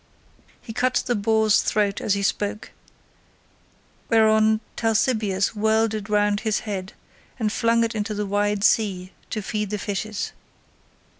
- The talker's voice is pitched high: Yes, high, 215 Hz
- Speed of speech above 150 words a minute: No, average, 140 wpm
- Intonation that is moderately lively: No, narrow, 1.4 semitones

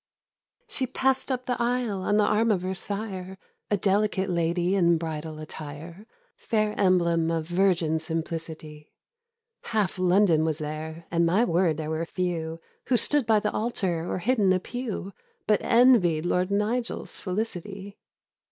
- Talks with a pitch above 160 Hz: Yes, medium, 185 Hz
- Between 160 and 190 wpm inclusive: No, average, 150 wpm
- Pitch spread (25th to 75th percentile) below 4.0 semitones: No, average, 4.3 semitones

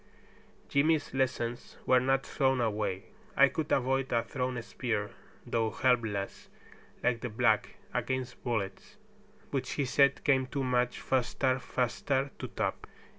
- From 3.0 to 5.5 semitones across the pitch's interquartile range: No, narrow, 2.4 semitones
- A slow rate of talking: Yes, slow, 130 wpm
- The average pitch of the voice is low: Yes, low, 125 Hz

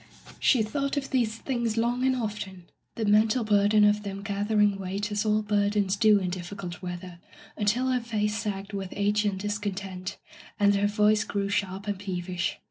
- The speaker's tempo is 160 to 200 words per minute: Yes, average, 180 wpm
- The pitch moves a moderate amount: No, narrow, 1.7 semitones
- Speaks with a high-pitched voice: Yes, high, 205 Hz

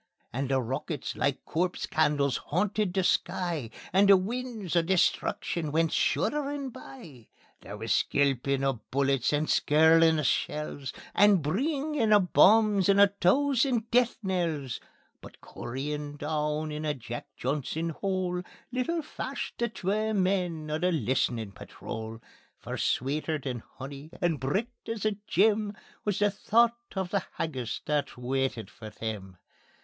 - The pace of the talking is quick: No, average, 145 wpm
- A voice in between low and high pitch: Yes, medium, 165 Hz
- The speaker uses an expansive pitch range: Yes, wide, 6.8 semitones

